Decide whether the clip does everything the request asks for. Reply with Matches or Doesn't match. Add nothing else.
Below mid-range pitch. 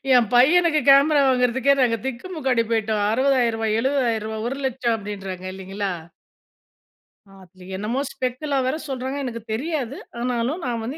Doesn't match